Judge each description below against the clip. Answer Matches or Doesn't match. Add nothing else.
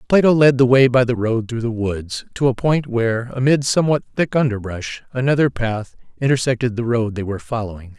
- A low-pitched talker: Matches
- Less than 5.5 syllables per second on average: Doesn't match